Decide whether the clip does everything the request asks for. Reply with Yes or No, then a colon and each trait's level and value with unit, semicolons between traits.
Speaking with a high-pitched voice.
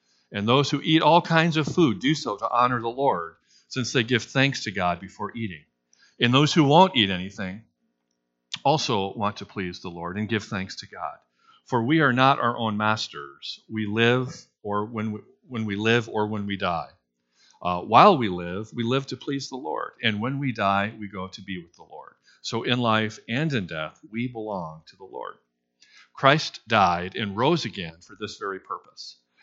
No: low, 110 Hz